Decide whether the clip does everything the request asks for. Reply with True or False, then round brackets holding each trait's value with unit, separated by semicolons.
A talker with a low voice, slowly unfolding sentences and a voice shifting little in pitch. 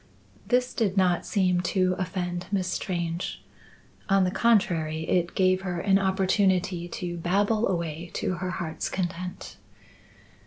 False (185 Hz; 130 wpm; 1.8 semitones)